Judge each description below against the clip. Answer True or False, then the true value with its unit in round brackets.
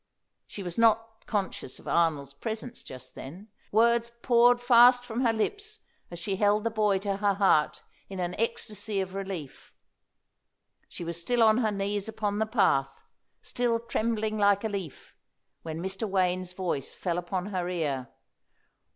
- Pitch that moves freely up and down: False (4.0 semitones)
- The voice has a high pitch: True (200 Hz)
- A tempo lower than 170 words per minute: True (160 wpm)